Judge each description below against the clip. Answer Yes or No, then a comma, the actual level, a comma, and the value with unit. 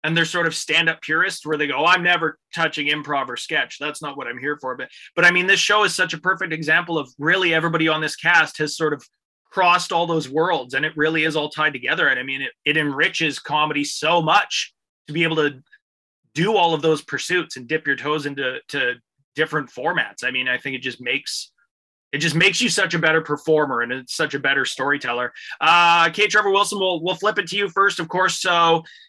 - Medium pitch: Yes, medium, 160 Hz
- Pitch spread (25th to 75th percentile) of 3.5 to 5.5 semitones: No, average, 2.9 semitones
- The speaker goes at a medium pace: No, fast, 235 wpm